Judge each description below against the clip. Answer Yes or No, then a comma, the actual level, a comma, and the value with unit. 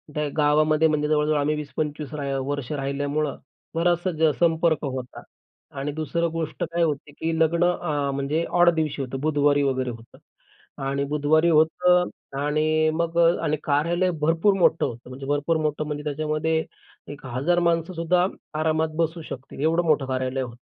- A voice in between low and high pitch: Yes, medium, 155 Hz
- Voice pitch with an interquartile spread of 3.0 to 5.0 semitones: No, narrow, 2.4 semitones